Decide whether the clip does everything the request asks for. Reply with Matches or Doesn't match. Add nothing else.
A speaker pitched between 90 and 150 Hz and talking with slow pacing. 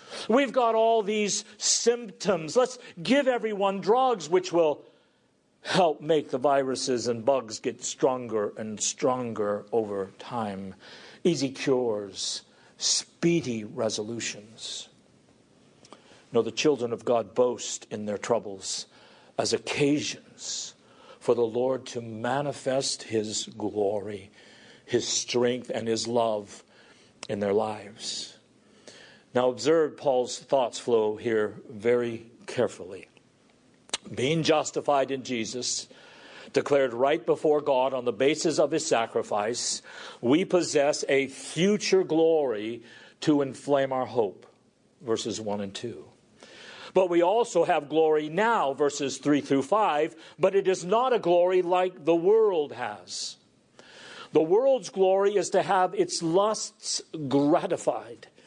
Matches